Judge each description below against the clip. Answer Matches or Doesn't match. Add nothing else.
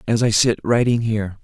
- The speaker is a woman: Doesn't match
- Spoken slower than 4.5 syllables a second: Doesn't match